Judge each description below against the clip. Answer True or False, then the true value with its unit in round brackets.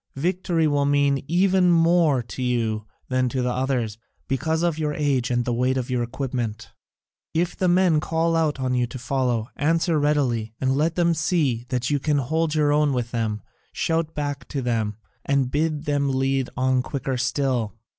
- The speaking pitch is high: False (135 Hz)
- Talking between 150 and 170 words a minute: False (185 wpm)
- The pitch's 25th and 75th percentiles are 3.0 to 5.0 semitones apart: True (4.1 semitones)